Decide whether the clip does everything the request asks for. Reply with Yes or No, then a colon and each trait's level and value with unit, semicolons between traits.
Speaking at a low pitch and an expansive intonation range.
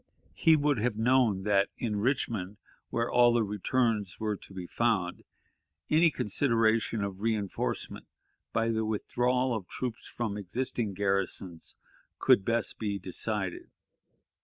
No: low, 110 Hz; average, 3.3 semitones